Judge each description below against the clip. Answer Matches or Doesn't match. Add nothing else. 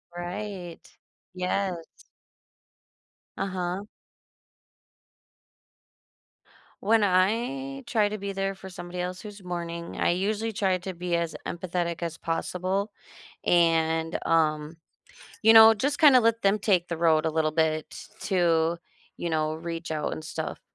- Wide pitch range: Doesn't match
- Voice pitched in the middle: Matches